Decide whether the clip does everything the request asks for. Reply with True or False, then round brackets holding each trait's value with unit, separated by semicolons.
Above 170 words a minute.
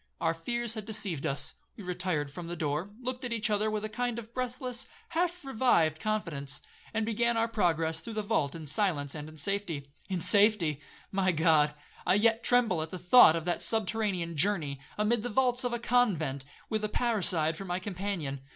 True (195 wpm)